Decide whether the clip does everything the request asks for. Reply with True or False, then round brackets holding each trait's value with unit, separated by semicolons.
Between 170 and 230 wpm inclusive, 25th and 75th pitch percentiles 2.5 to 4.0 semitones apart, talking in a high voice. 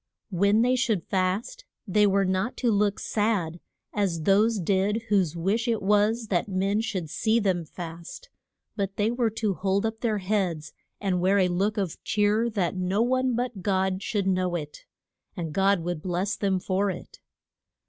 True (180 wpm; 2.8 semitones; 200 Hz)